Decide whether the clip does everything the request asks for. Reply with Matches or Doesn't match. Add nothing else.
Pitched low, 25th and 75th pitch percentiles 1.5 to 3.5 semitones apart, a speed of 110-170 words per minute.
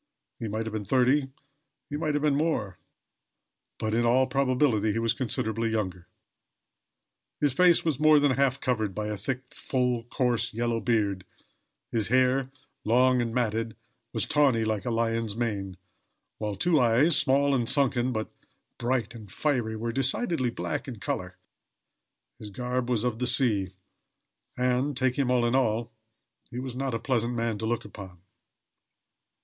Matches